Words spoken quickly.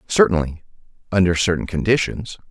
No: slow, 95 wpm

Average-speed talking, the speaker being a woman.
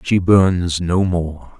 No: average, 150 wpm; male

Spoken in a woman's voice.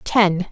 Yes: female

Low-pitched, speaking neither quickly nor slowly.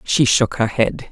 No: low, 120 Hz; fast, 215 wpm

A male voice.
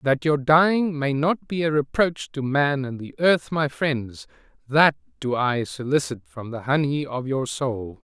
Yes: male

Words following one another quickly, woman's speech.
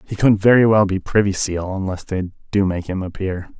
No: fast, 235 wpm; male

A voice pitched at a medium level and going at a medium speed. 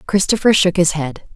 Yes: medium, 180 Hz; average, 175 wpm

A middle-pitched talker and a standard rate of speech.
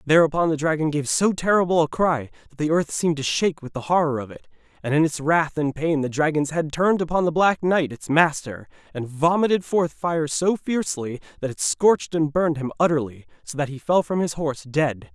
No: medium, 155 Hz; fast, 220 wpm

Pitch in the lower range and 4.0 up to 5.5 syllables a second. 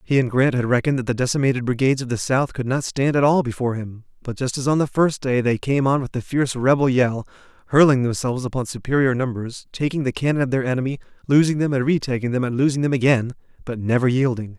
No: low, 130 Hz; 6.6 syllables/s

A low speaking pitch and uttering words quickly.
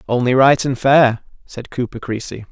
No: low, 125 Hz; average, 165 wpm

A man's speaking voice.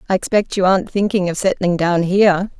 No: female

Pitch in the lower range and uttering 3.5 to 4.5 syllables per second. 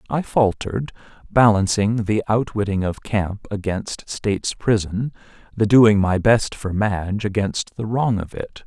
Yes: low, 105 Hz; 4.2 syllables/s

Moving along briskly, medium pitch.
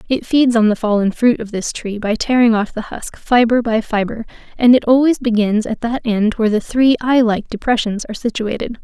No: fast, 215 wpm; high, 225 Hz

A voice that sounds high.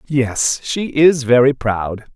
No: low, 130 Hz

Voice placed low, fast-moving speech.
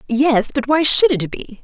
No: high, 245 Hz; fast, 220 wpm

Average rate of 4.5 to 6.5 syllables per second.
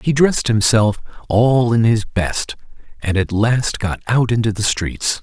No: 4.1 syllables/s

